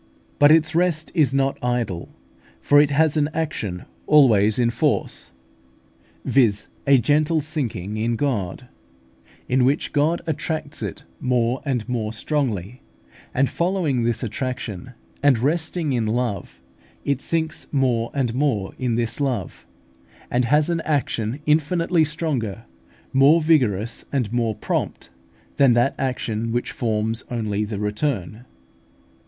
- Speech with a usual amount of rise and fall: Yes, average, 4.8 semitones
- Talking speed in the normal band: No, slow, 130 wpm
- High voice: No, low, 130 Hz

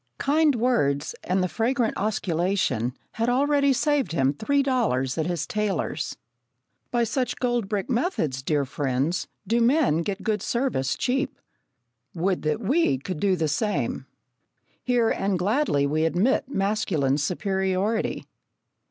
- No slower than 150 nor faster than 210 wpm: No, slow, 135 wpm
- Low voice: No, high, 200 Hz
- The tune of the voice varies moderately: No, wide, 7.7 semitones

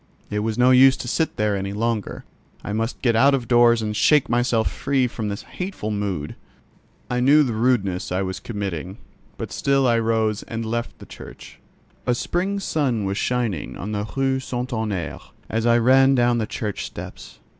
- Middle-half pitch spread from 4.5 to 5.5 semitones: No, average, 3.5 semitones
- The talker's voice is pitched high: No, low, 115 Hz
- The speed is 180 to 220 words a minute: Yes, average, 190 wpm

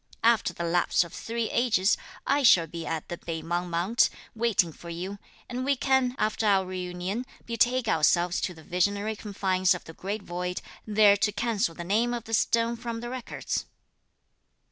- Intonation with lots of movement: No, average, 4.7 semitones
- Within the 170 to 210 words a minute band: Yes, average, 180 wpm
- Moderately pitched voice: No, high, 200 Hz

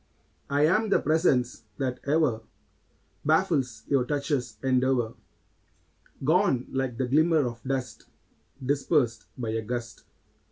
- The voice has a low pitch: Yes, low, 130 Hz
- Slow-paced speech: Yes, slow, 115 wpm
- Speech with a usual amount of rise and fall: Yes, average, 3.6 semitones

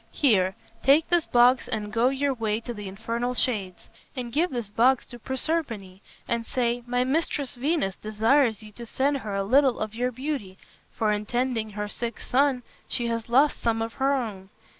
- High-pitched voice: Yes, high, 240 Hz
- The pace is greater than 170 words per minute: Yes, average, 185 wpm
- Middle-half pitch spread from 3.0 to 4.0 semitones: Yes, average, 3.5 semitones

